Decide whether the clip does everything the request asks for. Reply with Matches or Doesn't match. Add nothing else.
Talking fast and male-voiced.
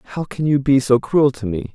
Matches